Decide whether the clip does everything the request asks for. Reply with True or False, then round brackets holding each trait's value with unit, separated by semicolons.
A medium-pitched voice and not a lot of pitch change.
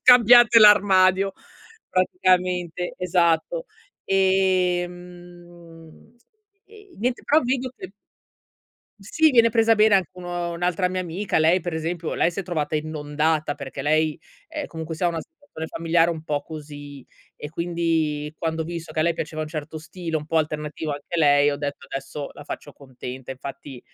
False (170 Hz; 3.3 semitones)